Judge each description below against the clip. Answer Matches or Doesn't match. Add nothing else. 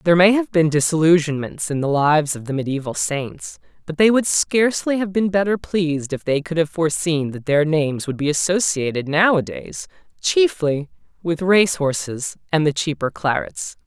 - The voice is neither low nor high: Matches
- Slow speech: Doesn't match